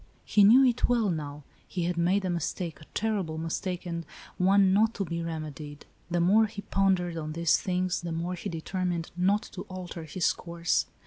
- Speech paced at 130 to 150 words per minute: No, average, 190 wpm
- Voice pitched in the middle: Yes, medium, 180 Hz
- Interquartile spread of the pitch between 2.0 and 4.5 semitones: Yes, average, 2.8 semitones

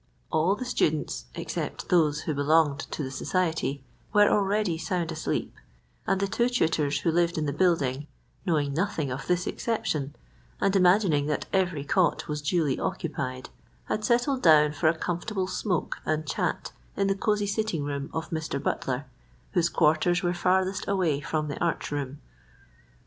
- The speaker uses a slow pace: No, average, 160 wpm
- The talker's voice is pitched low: No, medium, 165 Hz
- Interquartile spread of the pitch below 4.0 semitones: No, average, 4.4 semitones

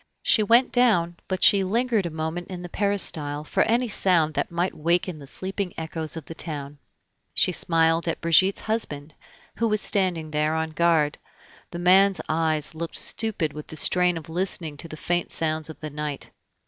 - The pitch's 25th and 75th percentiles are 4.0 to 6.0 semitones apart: No, average, 3.3 semitones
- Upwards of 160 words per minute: Yes, average, 185 wpm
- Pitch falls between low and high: Yes, medium, 170 Hz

